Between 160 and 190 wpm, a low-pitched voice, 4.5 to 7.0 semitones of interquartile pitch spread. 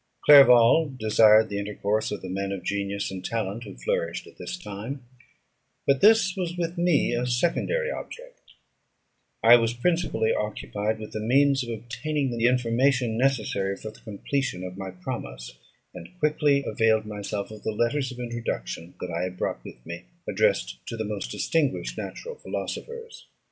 Yes: average, 165 wpm; low, 115 Hz; wide, 5.6 semitones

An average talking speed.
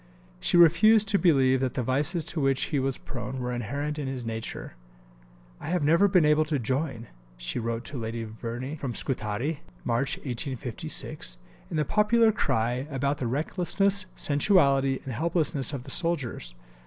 Yes: average, 165 wpm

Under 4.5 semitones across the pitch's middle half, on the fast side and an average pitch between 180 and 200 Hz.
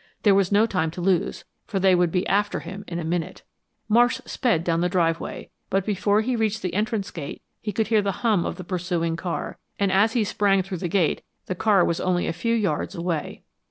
Yes: average, 3.3 semitones; fast, 225 wpm; high, 190 Hz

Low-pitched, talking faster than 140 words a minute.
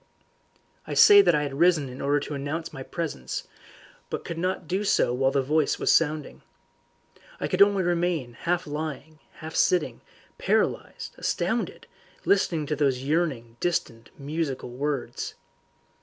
No: medium, 150 Hz; average, 150 wpm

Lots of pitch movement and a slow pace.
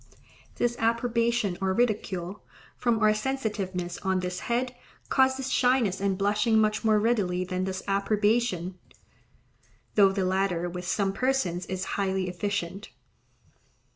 No: average, 3.9 semitones; slow, 120 wpm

